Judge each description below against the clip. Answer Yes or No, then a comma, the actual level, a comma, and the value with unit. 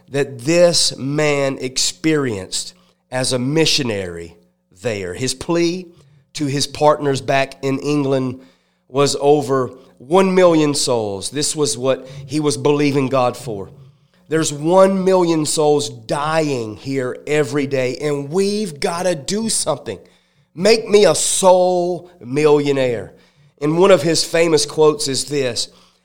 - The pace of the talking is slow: Yes, slow, 130 wpm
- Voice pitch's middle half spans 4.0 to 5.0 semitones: No, average, 3.4 semitones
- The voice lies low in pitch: No, medium, 145 Hz